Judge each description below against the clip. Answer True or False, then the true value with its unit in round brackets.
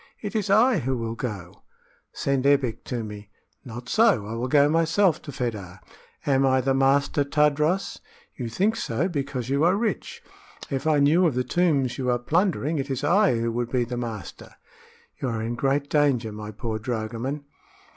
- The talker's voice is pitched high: False (135 Hz)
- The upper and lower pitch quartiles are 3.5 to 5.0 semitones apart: True (4.3 semitones)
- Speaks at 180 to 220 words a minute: True (185 wpm)